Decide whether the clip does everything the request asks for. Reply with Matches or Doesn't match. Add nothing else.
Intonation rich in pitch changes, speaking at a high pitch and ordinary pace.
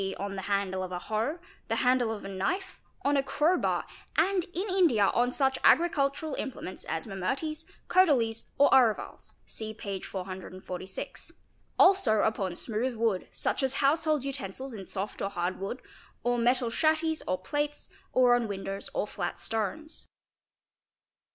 Matches